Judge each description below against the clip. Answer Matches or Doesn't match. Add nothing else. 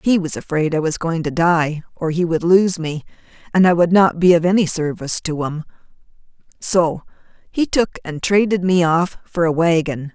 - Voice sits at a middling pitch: Matches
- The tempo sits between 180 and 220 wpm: Matches